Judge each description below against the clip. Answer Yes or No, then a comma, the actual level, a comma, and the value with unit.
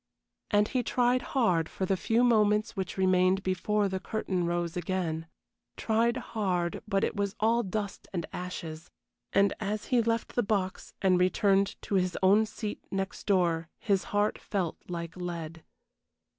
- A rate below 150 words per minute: No, average, 155 wpm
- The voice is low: No, high, 195 Hz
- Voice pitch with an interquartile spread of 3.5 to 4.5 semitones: No, average, 3.1 semitones